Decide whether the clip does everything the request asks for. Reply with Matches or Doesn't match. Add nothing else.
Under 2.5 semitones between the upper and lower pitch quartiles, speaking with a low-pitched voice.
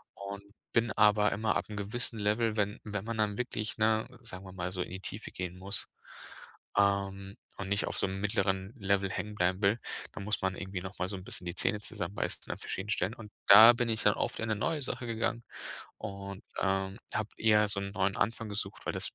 Matches